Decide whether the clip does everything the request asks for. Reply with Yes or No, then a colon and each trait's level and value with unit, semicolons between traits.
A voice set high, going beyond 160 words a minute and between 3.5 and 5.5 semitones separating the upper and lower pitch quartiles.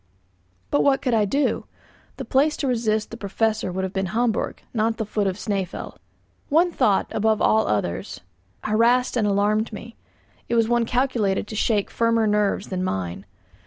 No: high, 220 Hz; average, 170 wpm; average, 2.8 semitones